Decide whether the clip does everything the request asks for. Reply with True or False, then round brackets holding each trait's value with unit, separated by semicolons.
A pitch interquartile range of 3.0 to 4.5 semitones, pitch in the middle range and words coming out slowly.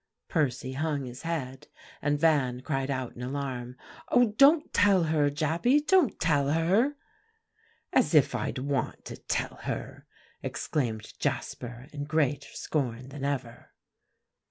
True (3.9 semitones; 145 Hz; 130 wpm)